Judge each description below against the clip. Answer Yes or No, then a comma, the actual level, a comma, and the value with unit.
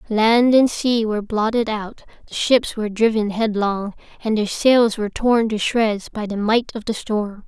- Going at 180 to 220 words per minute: Yes, average, 195 wpm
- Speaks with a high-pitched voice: Yes, high, 220 Hz